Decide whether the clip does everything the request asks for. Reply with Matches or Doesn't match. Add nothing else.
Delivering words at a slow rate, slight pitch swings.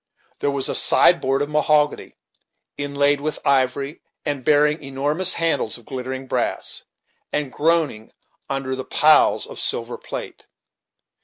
Matches